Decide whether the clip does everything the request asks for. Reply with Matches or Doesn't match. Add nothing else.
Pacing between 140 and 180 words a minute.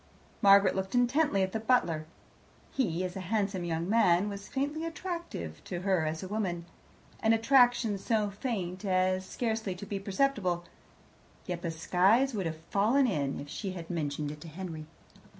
Matches